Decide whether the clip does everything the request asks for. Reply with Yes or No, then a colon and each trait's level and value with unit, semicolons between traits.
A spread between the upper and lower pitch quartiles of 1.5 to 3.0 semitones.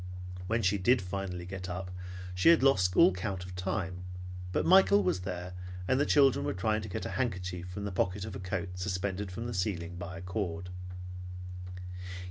Yes: narrow, 2.6 semitones